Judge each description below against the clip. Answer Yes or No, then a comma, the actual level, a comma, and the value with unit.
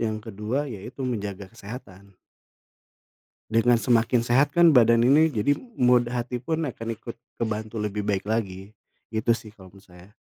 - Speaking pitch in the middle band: No, low, 115 Hz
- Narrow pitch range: No, average, 3.1 semitones